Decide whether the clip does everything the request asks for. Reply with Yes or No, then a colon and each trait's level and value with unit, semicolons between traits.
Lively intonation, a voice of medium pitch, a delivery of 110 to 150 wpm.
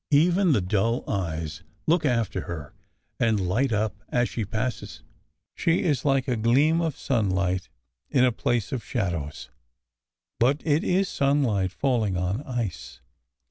No: wide, 6.3 semitones; low, 120 Hz; average, 145 wpm